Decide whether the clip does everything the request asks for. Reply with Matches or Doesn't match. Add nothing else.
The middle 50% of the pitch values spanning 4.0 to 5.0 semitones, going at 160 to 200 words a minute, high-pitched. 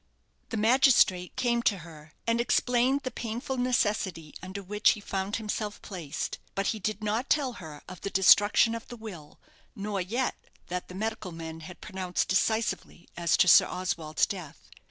Matches